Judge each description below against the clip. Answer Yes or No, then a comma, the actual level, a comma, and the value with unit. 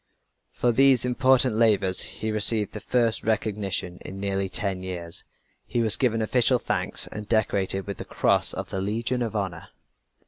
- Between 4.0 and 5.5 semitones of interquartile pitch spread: No, average, 3.4 semitones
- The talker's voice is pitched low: Yes, low, 110 Hz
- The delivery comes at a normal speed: Yes, average, 165 wpm